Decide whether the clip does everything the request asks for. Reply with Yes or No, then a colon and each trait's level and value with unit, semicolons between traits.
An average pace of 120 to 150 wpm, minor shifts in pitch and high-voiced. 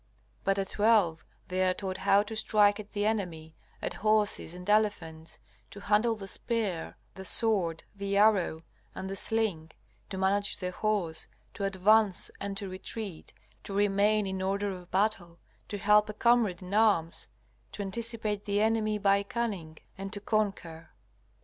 No: average, 160 wpm; narrow, 2.3 semitones; high, 200 Hz